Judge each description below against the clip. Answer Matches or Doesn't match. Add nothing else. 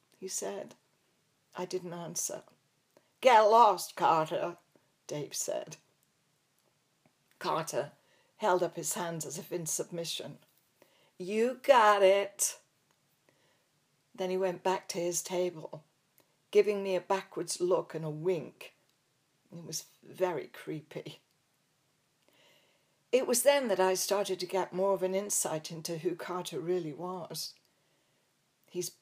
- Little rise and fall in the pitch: Matches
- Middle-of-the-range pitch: Matches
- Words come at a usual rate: Doesn't match